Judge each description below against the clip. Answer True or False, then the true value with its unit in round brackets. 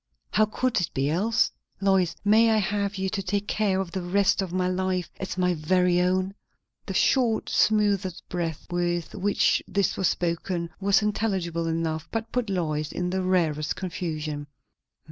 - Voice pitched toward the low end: False (185 Hz)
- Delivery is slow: False (165 wpm)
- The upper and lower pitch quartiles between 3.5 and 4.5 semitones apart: False (2.9 semitones)